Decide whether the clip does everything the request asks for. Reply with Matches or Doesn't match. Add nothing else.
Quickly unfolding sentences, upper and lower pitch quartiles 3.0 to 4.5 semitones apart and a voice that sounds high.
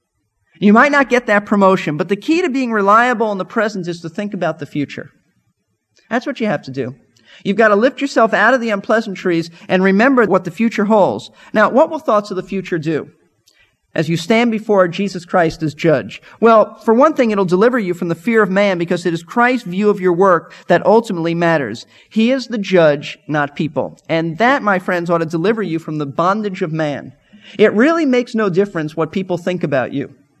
Doesn't match